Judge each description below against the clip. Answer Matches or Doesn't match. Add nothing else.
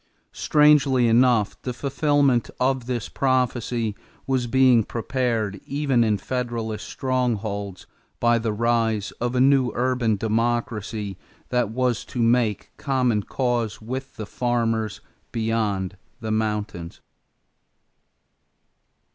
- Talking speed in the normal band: Doesn't match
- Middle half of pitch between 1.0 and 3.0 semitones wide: Matches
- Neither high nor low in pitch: Doesn't match